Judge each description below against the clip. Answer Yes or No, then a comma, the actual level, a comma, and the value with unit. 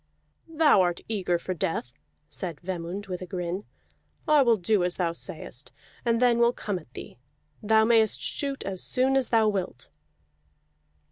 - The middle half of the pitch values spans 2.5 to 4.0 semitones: No, average, 4.9 semitones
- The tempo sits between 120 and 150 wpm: No, average, 160 wpm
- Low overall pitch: No, high, 200 Hz